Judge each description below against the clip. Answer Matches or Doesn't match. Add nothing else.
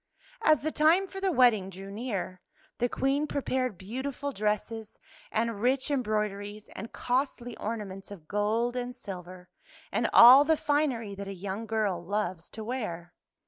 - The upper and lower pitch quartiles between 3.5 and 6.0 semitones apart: Matches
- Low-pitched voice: Doesn't match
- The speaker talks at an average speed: Matches